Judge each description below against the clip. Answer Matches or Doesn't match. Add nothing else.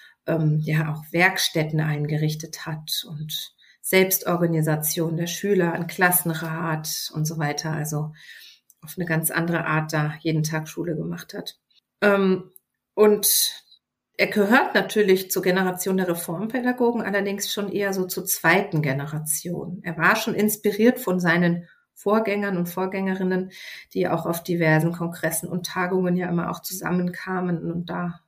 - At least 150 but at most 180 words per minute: Doesn't match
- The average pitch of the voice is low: Doesn't match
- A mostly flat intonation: Doesn't match